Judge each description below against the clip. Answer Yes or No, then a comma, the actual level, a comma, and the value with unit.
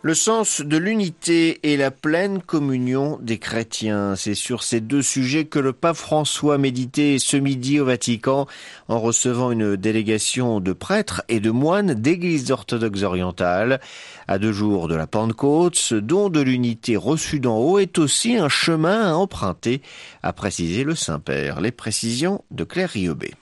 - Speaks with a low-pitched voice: Yes, low, 130 Hz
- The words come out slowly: No, average, 165 wpm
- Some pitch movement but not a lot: No, wide, 6.0 semitones